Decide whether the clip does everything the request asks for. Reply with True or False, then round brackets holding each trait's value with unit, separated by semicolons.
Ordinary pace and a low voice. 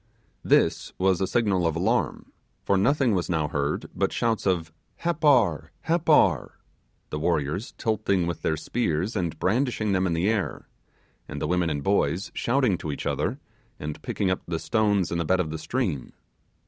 True (175 wpm; 95 Hz)